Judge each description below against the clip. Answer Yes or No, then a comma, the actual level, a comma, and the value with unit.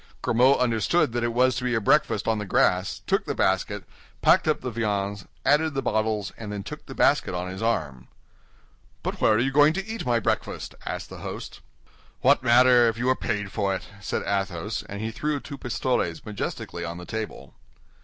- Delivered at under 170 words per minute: No, fast, 205 wpm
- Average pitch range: Yes, average, 4.2 semitones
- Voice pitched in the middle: No, low, 110 Hz